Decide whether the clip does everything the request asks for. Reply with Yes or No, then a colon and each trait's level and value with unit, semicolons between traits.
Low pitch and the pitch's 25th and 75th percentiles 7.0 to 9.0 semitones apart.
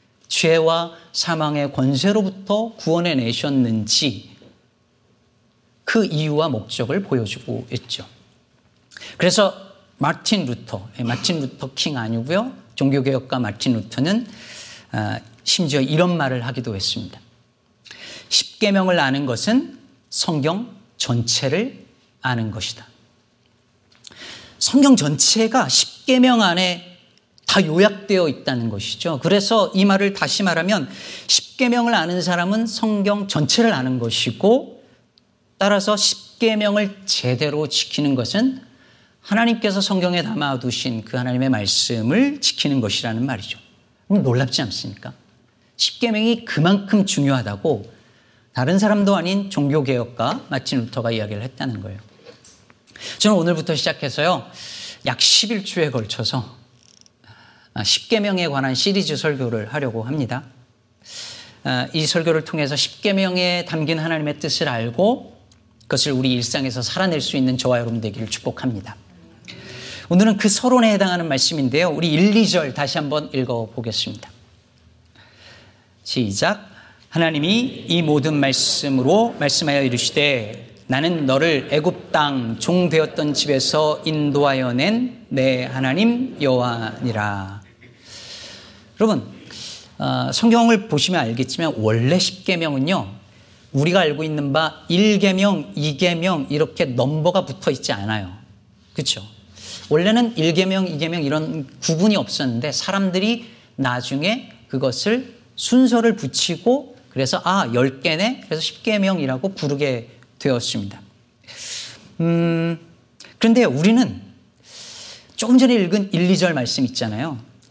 No: medium, 145 Hz; wide, 7.7 semitones